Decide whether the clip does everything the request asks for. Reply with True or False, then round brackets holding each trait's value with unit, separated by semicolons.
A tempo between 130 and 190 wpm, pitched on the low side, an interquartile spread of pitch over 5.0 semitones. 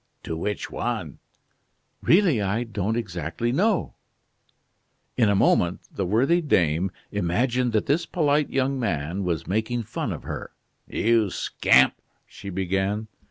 True (135 wpm; 110 Hz; 5.4 semitones)